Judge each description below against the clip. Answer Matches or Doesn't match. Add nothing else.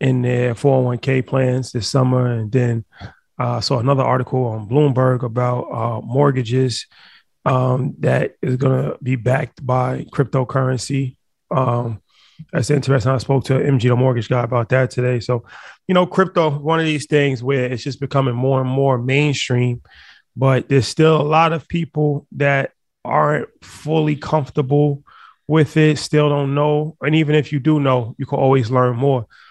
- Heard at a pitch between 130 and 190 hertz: Matches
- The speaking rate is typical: Matches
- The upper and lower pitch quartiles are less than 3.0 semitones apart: Matches